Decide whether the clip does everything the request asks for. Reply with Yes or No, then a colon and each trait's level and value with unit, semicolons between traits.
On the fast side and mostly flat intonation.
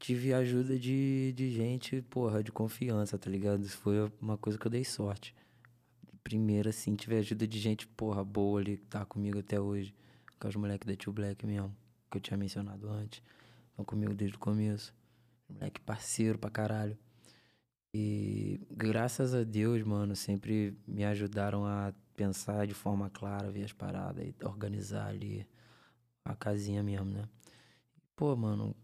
No: average, 160 wpm; narrow, 2.3 semitones